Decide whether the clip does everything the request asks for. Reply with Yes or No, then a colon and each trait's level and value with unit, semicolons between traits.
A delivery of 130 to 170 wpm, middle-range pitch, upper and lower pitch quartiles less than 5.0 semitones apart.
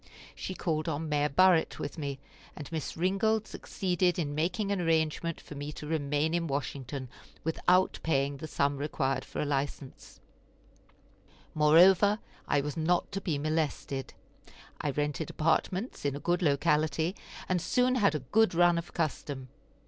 Yes: average, 155 wpm; medium, 155 Hz; average, 3.6 semitones